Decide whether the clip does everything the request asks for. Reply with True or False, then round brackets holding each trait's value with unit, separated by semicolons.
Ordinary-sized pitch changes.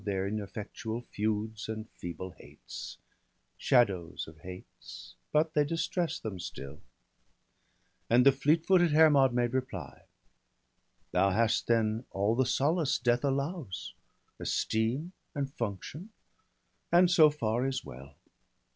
False (6.1 semitones)